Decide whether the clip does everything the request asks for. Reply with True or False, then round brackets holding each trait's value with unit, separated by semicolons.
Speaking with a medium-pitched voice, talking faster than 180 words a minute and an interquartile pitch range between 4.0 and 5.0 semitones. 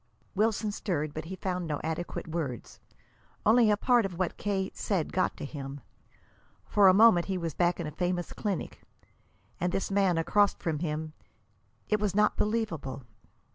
False (180 Hz; 170 wpm; 4.3 semitones)